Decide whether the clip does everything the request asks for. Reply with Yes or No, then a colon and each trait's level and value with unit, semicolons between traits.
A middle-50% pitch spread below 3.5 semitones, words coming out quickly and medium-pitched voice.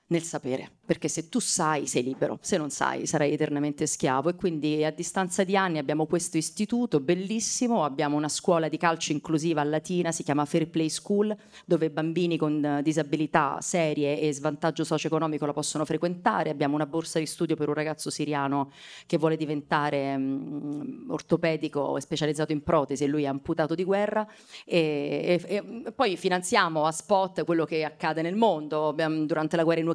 Yes: narrow, 2.4 semitones; fast, 180 wpm; medium, 160 Hz